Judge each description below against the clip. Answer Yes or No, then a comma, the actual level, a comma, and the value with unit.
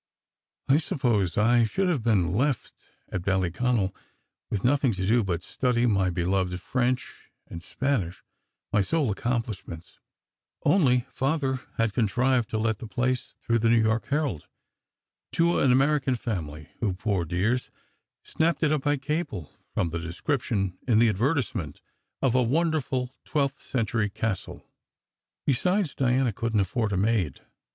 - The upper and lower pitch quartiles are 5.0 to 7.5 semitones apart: Yes, wide, 5.5 semitones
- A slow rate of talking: No, average, 145 wpm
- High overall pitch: No, low, 115 Hz